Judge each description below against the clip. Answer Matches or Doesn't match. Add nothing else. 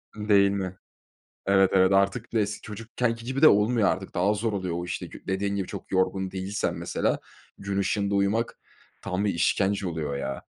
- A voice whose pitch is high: Doesn't match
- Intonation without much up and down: Matches